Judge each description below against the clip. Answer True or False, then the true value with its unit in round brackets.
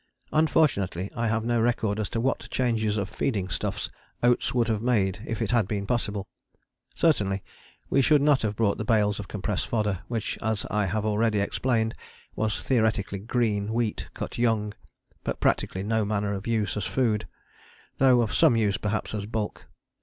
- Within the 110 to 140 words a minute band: False (180 wpm)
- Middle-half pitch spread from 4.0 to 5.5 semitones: False (2.5 semitones)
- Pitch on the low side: True (110 Hz)